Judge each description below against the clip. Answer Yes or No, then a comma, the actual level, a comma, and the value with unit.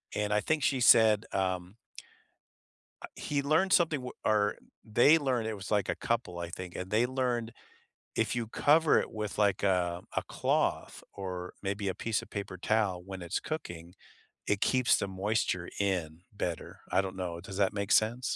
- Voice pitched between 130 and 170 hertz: No, low, 105 Hz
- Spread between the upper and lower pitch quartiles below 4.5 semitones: No, average, 4.9 semitones